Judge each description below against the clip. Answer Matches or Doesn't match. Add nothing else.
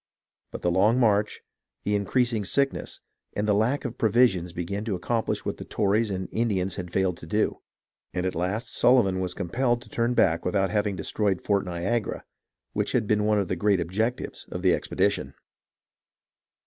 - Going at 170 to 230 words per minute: Matches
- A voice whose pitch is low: Matches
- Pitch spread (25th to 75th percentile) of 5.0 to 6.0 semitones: Doesn't match